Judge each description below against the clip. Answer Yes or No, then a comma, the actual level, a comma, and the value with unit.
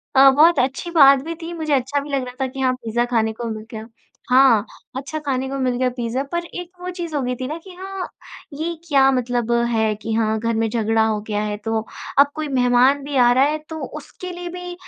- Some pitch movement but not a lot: Yes, average, 4.9 semitones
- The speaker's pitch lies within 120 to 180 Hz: No, very high, 265 Hz